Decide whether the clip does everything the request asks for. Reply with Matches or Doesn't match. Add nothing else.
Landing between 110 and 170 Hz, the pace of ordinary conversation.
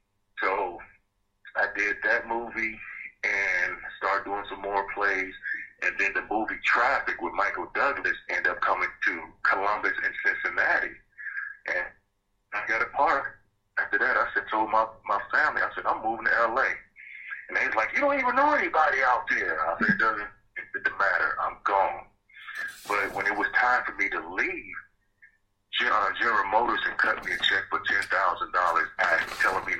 Doesn't match